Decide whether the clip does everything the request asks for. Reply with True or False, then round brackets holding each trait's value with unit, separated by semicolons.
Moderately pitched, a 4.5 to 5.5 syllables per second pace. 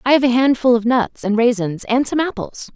False (240 Hz; 5.3 syllables/s)